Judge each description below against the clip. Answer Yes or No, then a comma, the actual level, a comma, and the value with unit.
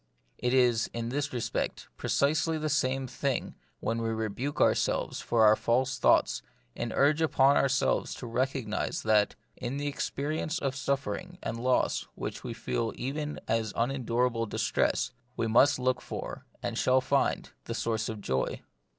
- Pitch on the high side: No, low, 130 Hz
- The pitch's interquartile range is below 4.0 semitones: Yes, average, 3.3 semitones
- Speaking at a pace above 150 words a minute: Yes, average, 160 wpm